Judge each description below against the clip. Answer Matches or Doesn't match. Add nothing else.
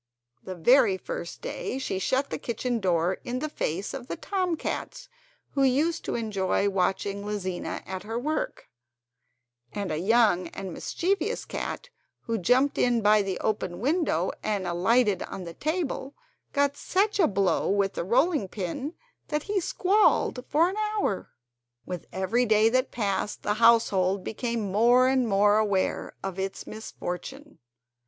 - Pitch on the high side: Matches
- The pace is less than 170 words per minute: Matches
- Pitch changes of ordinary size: Doesn't match